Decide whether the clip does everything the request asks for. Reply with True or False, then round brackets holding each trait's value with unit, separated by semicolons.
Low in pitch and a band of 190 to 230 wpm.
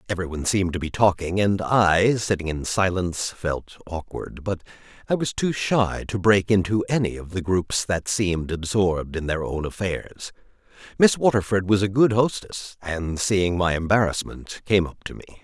False (95 Hz; 175 wpm)